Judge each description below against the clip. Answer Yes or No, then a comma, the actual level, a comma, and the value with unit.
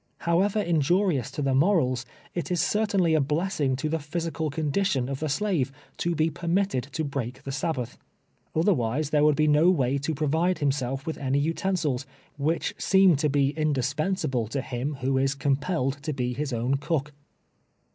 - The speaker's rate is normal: Yes, average, 175 wpm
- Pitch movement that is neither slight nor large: Yes, average, 3.7 semitones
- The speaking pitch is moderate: Yes, medium, 150 Hz